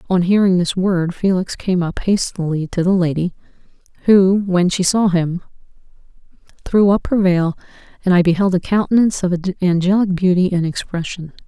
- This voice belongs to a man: No, female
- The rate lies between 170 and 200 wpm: No, average, 155 wpm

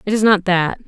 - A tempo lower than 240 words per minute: No, fast, 275 wpm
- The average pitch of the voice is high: Yes, high, 195 Hz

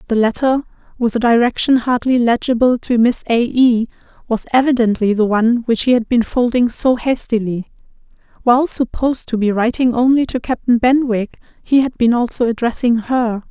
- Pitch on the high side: Yes, high, 240 Hz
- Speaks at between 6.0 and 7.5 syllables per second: No, 5.3 syllables/s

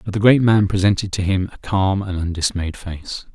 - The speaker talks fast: Yes, fast, 215 wpm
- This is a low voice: Yes, very low, 95 Hz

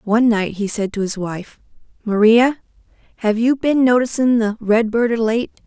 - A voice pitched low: No, high, 225 Hz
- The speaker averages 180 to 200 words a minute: No, average, 170 wpm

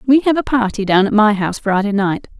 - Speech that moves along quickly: Yes, fast, 250 wpm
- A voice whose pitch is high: Yes, high, 220 Hz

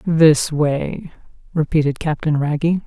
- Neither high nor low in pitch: Yes, medium, 155 Hz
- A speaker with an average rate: No, slow, 105 wpm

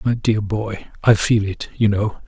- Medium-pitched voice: No, low, 105 Hz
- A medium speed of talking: No, fast, 210 wpm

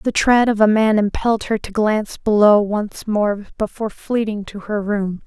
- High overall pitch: Yes, high, 210 Hz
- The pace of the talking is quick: No, average, 195 wpm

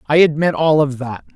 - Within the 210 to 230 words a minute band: Yes, fast, 220 wpm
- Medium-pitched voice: Yes, medium, 150 Hz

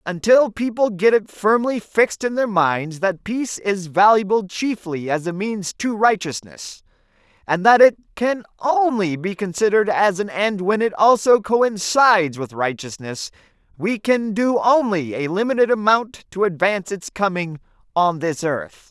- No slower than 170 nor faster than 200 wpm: No, average, 155 wpm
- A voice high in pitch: Yes, high, 200 Hz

